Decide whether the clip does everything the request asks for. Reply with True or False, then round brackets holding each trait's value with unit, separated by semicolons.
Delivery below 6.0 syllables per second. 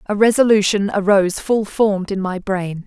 True (5.1 syllables/s)